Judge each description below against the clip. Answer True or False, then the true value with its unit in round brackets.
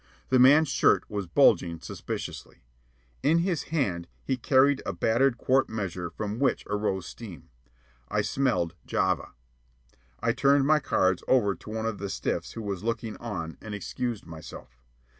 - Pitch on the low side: True (110 Hz)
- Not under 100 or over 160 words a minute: True (155 wpm)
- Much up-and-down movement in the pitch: True (5.9 semitones)